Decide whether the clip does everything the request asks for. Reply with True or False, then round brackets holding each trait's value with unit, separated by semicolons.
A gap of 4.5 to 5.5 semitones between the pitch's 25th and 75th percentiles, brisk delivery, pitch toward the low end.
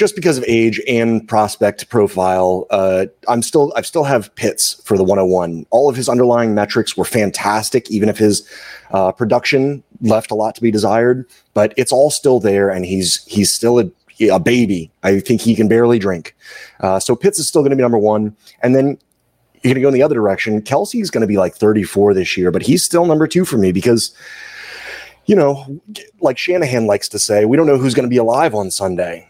True (5.0 semitones; 215 wpm; 115 Hz)